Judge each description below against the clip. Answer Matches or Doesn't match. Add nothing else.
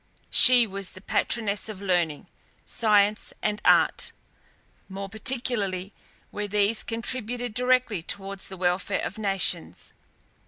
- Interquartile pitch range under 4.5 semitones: Matches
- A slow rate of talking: Matches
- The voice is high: Matches